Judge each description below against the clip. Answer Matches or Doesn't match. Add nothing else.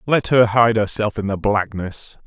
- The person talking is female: Doesn't match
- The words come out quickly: Doesn't match